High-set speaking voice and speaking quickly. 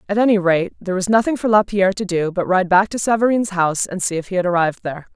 Yes: high, 195 Hz; fast, 270 wpm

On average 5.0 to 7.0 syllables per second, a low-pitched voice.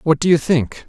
No: 5.2 syllables/s; medium, 150 Hz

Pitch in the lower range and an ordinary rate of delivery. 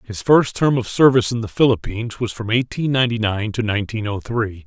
No: low, 115 Hz; fast, 220 wpm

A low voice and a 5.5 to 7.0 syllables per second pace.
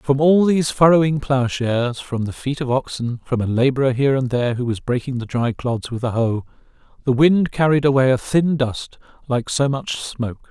No: low, 130 Hz; 5.2 syllables/s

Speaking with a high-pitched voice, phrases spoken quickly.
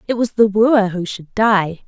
Yes: high, 205 Hz; fast, 225 wpm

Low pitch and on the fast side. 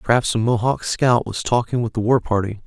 Yes: low, 115 Hz; fast, 225 wpm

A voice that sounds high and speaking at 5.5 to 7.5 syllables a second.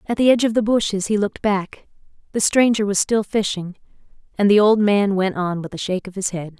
Yes: high, 200 Hz; 5.9 syllables/s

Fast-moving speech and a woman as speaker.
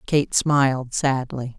No: slow, 115 wpm; female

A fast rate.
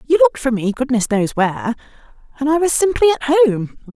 No: average, 195 wpm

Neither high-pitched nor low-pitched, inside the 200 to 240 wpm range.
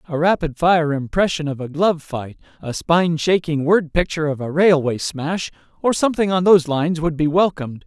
No: medium, 160 Hz; average, 190 wpm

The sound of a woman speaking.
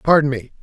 No: male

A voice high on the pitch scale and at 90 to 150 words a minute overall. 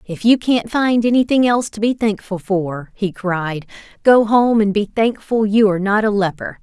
No: high, 210 Hz; average, 200 wpm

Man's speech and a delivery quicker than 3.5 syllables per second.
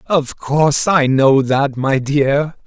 No: male; 3.2 syllables/s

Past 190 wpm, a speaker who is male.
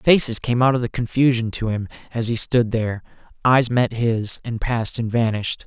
Yes: average, 200 wpm; male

